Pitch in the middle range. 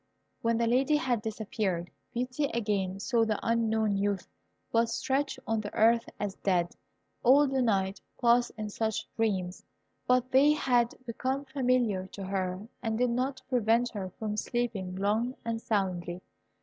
No: high, 225 Hz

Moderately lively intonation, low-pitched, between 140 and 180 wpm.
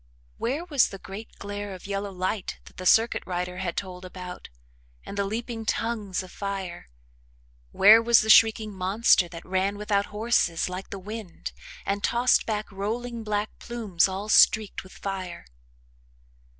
No: average, 3.0 semitones; high, 200 Hz; average, 155 wpm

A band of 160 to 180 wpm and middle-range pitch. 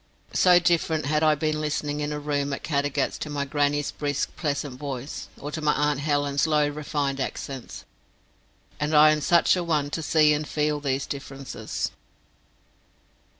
Yes: average, 165 wpm; medium, 150 Hz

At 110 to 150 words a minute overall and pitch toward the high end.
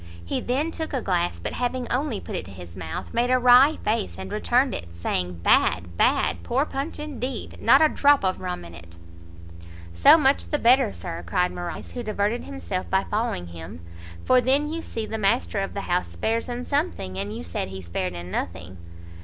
No: fast, 205 wpm; high, 210 Hz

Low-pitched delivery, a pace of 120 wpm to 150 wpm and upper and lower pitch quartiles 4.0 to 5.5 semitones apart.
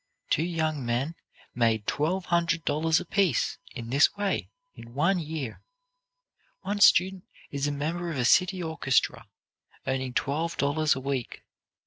No: medium, 155 Hz; average, 140 wpm; average, 4.3 semitones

